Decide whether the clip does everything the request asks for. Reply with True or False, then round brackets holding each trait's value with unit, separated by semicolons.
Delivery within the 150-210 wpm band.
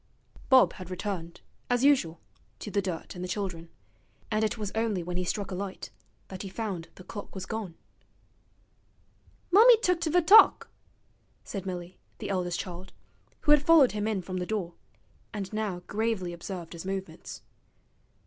True (165 wpm)